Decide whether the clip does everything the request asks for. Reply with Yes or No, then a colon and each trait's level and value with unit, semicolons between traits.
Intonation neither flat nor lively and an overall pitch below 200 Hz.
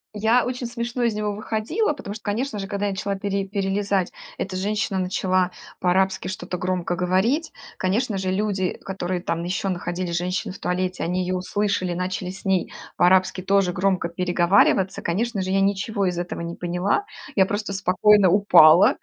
No: narrow, 2.1 semitones; high, 190 Hz